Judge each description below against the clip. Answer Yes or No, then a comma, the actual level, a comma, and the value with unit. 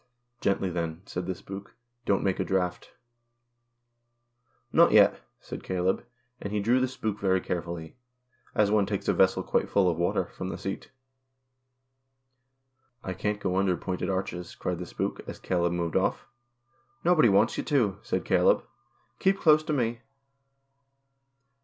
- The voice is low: Yes, low, 100 Hz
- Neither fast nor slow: Yes, average, 170 wpm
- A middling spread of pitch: Yes, average, 4.7 semitones